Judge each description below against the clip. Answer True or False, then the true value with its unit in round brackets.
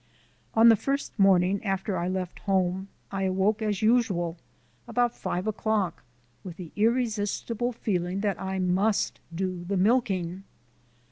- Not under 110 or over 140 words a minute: True (135 wpm)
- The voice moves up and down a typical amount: True (3.0 semitones)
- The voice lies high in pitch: True (195 Hz)